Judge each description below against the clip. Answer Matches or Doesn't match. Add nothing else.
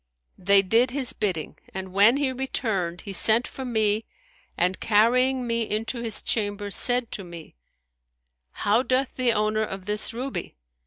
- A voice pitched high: Matches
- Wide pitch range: Doesn't match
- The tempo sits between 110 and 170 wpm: Matches